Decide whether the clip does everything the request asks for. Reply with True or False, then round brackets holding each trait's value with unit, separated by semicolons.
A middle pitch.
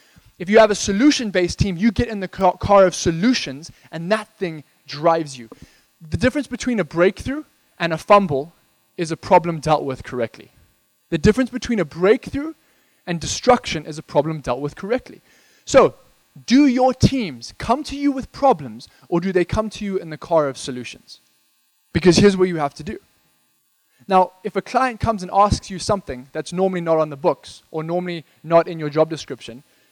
True (180 Hz)